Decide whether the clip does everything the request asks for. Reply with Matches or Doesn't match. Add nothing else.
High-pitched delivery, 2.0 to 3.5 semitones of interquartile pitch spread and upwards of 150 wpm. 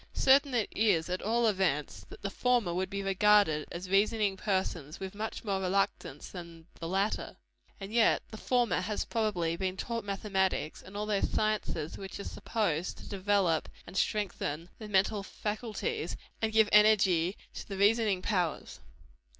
Matches